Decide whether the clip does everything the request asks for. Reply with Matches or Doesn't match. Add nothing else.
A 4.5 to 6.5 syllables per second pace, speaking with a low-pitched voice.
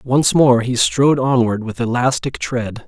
Doesn't match